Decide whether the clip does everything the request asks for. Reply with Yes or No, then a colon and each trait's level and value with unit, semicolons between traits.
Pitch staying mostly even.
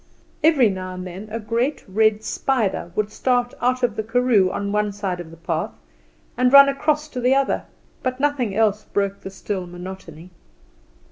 No: average, 4.8 semitones